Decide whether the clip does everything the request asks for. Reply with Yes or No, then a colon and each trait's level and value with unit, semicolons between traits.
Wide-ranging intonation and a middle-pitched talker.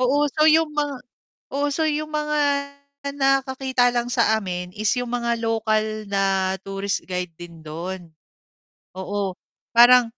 No: wide, 5.8 semitones; high, 230 Hz